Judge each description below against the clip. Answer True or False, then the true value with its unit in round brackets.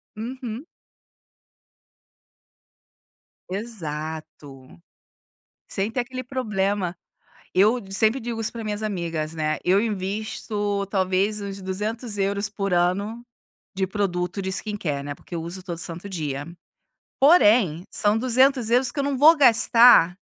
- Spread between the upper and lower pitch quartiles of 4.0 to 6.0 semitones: True (4.3 semitones)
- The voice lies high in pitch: True (205 Hz)